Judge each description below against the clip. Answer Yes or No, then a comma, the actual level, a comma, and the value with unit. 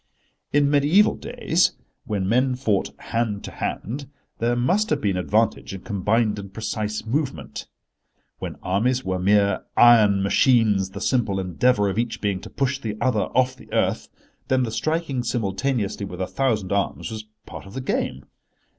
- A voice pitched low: Yes, low, 110 Hz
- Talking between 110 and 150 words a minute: No, average, 165 wpm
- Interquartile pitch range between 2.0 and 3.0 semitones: No, average, 4.4 semitones